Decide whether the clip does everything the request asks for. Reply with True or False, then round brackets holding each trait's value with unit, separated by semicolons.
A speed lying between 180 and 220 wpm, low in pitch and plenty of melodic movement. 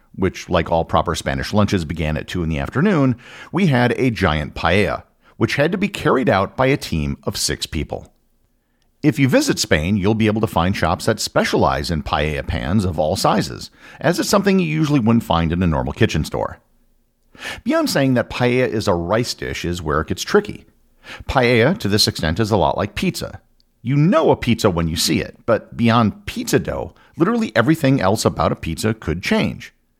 True (200 wpm; 110 Hz; 7.0 semitones)